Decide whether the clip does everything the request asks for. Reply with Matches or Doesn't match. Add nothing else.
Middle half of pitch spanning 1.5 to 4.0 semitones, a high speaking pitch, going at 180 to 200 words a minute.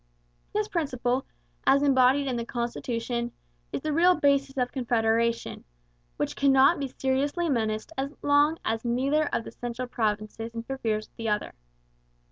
Doesn't match